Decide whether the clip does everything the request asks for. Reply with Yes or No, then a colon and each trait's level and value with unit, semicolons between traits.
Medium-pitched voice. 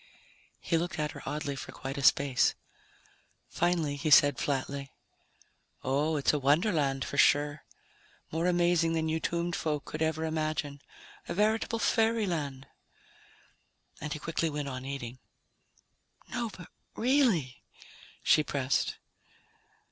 Yes: medium, 155 Hz